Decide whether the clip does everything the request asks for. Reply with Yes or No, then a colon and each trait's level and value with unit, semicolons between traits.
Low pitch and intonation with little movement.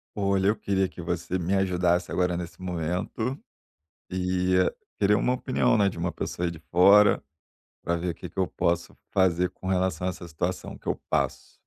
Yes: very low, 90 Hz; narrow, 1.9 semitones